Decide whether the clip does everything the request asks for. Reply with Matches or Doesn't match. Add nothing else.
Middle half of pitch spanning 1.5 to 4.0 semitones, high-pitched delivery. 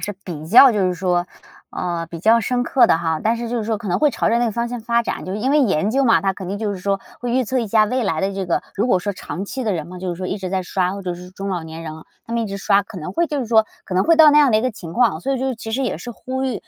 Doesn't match